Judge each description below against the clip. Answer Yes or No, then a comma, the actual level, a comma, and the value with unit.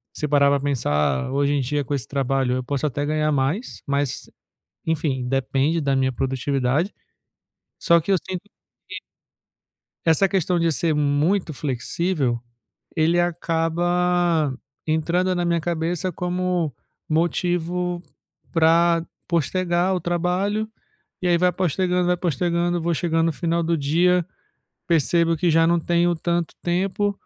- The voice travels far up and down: No, average, 3.6 semitones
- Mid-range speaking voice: Yes, medium, 165 Hz